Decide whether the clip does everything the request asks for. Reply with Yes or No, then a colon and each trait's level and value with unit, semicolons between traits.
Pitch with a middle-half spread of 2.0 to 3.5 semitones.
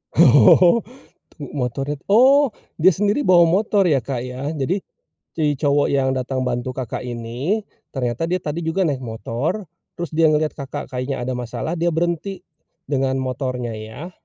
No: average, 5.1 semitones